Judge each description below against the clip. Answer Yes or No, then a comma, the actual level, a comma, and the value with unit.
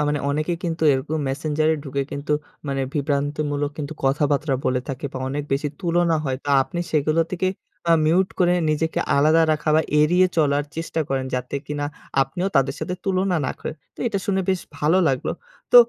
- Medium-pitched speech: Yes, medium, 150 Hz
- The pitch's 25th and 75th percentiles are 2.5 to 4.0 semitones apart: Yes, average, 2.9 semitones